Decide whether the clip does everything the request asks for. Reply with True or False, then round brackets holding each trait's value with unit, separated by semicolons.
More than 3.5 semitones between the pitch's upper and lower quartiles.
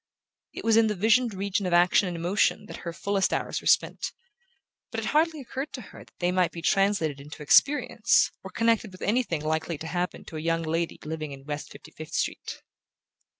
True (5.2 semitones)